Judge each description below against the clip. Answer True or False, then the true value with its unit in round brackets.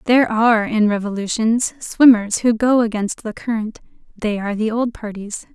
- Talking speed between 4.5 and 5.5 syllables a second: True (5.1 syllables/s)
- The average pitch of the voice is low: False (225 Hz)